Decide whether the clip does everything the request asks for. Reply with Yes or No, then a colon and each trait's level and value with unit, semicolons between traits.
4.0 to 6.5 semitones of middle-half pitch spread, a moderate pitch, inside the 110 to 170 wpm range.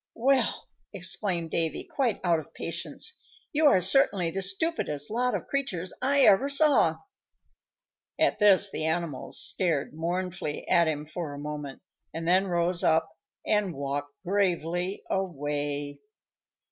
Yes: average, 4.7 semitones; medium, 175 Hz; slow, 135 wpm